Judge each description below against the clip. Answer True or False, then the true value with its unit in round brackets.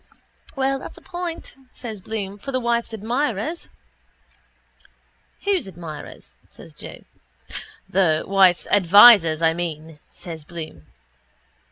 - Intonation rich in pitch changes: True (6.5 semitones)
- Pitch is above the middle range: True (195 Hz)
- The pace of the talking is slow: True (110 wpm)